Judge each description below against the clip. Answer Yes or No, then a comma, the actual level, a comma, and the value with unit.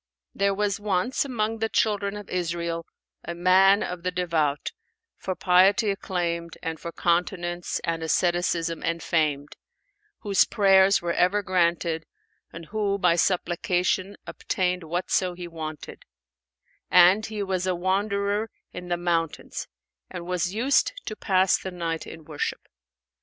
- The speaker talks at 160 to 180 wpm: No, slow, 135 wpm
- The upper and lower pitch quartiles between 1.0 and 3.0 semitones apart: Yes, average, 2.7 semitones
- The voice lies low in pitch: No, medium, 180 Hz